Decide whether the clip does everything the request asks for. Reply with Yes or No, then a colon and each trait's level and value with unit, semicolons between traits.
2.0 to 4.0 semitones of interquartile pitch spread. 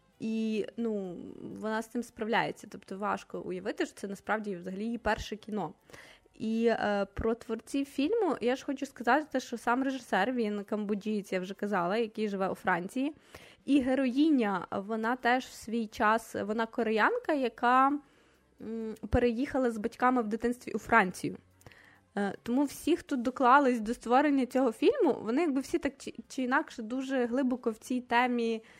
Yes: average, 3.4 semitones